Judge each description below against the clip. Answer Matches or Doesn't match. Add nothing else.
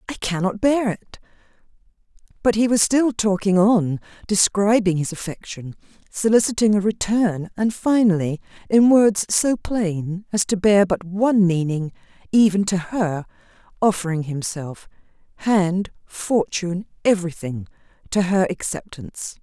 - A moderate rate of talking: Doesn't match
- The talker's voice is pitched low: Doesn't match